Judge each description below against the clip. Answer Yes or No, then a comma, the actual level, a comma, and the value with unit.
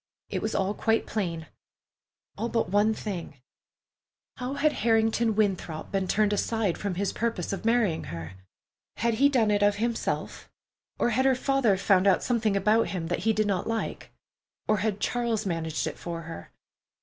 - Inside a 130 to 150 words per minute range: No, average, 170 wpm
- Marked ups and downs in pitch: No, average, 3.6 semitones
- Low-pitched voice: No, high, 210 Hz